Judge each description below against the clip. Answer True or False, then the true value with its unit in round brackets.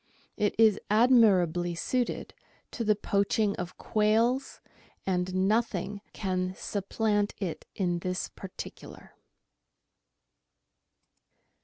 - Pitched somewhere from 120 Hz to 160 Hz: False (200 Hz)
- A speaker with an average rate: False (90 wpm)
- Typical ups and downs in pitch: True (3.1 semitones)